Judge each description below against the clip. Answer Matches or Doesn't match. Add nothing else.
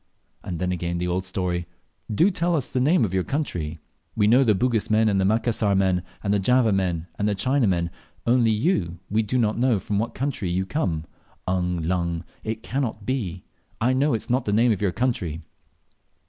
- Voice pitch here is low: Matches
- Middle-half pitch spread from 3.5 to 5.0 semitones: Doesn't match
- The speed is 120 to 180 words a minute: Doesn't match